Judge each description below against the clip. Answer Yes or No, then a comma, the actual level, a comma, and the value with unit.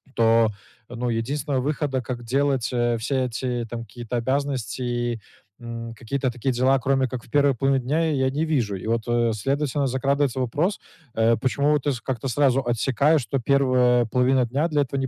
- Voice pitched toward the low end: Yes, low, 130 Hz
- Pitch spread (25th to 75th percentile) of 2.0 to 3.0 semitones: Yes, average, 2.7 semitones